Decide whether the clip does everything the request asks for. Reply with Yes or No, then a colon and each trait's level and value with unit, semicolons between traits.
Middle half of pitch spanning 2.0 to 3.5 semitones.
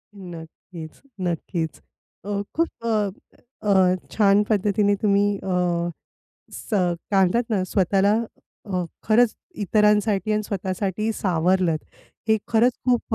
Yes: average, 2.8 semitones